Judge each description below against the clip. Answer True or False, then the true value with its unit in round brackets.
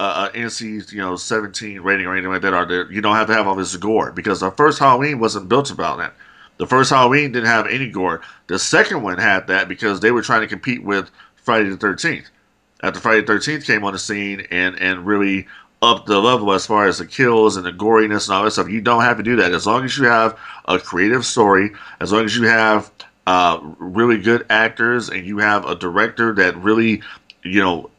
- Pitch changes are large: False (3.0 semitones)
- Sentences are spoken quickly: True (230 wpm)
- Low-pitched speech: True (105 Hz)